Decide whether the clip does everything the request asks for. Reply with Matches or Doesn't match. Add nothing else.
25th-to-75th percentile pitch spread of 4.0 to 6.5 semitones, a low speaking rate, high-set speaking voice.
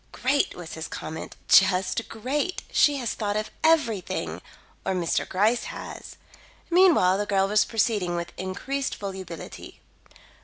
Matches